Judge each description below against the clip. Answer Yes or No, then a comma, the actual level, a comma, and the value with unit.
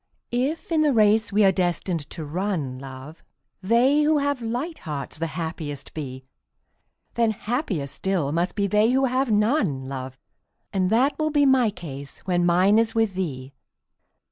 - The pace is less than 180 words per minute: Yes, average, 165 wpm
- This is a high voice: Yes, high, 195 Hz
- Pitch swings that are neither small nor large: No, wide, 7.8 semitones